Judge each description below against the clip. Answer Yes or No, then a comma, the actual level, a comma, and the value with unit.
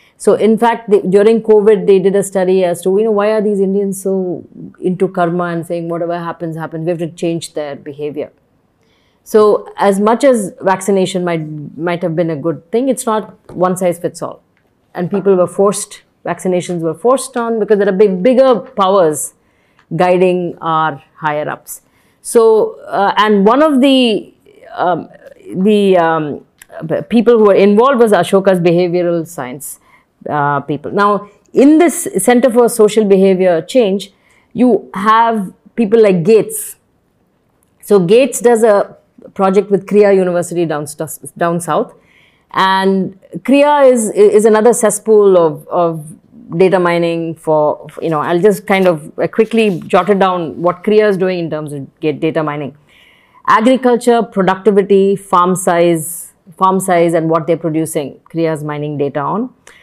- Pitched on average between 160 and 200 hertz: Yes, high, 190 Hz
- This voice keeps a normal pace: Yes, average, 160 wpm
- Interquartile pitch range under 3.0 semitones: No, average, 4.2 semitones